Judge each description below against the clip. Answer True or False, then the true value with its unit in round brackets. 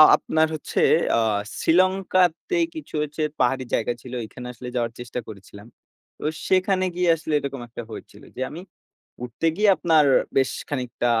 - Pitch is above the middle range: False (150 Hz)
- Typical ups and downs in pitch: False (6.4 semitones)